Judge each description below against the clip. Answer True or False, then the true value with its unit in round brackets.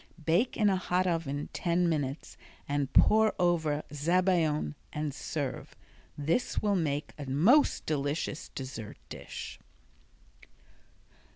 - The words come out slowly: True (110 wpm)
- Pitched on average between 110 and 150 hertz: False (160 Hz)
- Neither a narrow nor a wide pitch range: True (3.9 semitones)